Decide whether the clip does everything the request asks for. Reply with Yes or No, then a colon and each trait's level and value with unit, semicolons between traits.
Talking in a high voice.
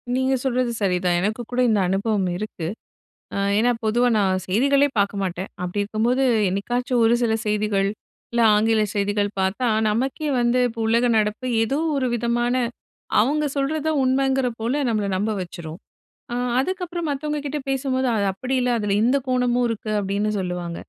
Yes: high, 230 Hz